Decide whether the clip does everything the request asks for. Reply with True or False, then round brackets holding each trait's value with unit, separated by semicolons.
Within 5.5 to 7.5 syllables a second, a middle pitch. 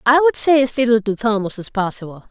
False (6.0 syllables/s; 235 Hz)